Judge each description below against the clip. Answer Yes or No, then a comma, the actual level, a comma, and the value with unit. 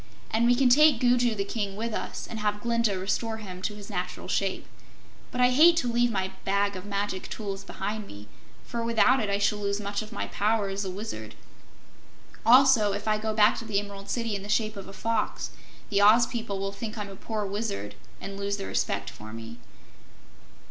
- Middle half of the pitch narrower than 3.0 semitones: Yes, narrow, 2.6 semitones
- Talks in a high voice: Yes, high, 210 Hz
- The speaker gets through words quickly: Yes, fast, 215 wpm